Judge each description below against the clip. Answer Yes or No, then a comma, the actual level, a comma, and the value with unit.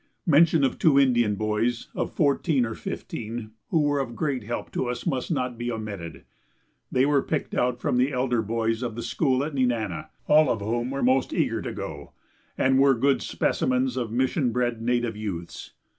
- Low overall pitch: Yes, low, 125 Hz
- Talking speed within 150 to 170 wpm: No, average, 190 wpm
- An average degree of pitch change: Yes, average, 3.0 semitones